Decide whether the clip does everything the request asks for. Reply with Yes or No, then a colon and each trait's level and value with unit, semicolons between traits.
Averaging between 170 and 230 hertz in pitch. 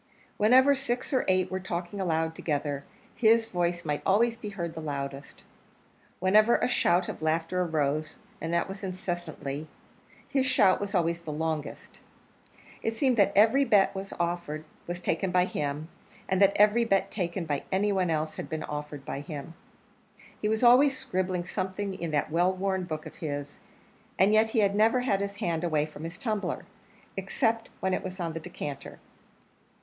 Yes: medium, 185 Hz